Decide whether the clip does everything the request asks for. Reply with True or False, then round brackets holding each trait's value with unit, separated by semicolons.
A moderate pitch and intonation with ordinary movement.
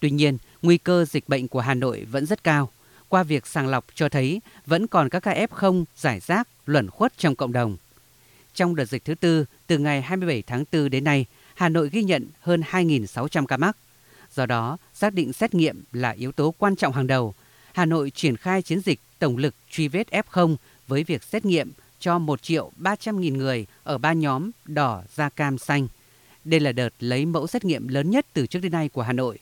True (150 Hz; 4.8 semitones)